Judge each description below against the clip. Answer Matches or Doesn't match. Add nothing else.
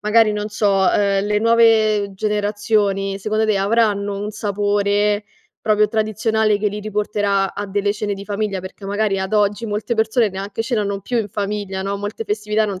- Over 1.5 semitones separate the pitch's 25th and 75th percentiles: Doesn't match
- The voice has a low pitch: Doesn't match